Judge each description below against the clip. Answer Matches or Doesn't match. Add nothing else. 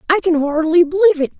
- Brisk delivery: Matches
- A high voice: Matches